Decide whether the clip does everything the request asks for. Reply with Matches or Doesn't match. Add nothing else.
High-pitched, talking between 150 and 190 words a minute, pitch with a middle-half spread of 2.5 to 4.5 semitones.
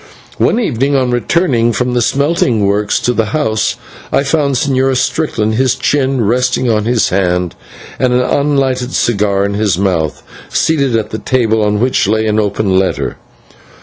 Doesn't match